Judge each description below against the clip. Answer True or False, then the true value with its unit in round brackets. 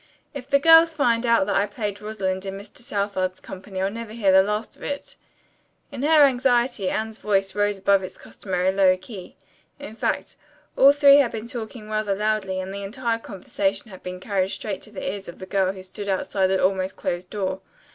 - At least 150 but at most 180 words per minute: False (205 wpm)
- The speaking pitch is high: True (205 Hz)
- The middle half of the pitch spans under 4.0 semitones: True (3.3 semitones)